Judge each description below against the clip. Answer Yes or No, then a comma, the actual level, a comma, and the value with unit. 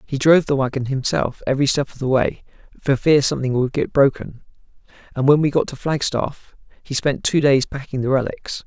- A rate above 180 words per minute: Yes, average, 200 wpm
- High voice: No, low, 135 Hz